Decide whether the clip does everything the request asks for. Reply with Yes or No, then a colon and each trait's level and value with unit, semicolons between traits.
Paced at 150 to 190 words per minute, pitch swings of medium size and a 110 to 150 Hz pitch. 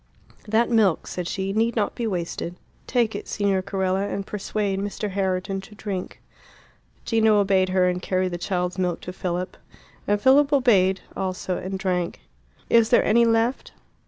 No: average, 160 wpm; average, 3.0 semitones; high, 195 Hz